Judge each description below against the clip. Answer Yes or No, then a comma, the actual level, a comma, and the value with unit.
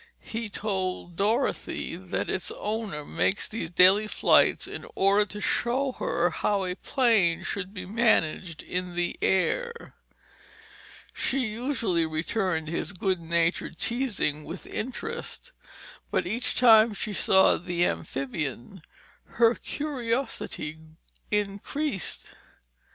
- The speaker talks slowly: Yes, slow, 110 wpm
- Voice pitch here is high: Yes, high, 195 Hz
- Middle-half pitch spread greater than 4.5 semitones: Yes, average, 4.9 semitones